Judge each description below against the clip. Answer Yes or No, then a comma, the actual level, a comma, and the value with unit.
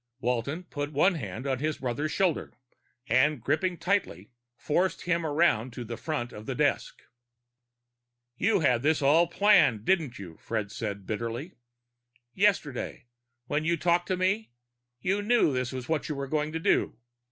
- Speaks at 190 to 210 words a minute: No, average, 160 wpm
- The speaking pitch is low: No, medium, 150 Hz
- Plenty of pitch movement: Yes, wide, 5.9 semitones